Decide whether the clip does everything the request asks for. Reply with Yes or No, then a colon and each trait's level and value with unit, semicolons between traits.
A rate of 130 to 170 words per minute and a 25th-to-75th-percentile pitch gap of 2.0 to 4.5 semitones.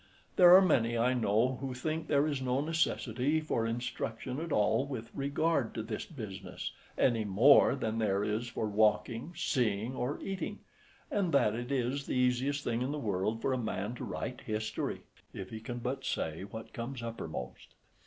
No: average, 180 wpm; average, 4.0 semitones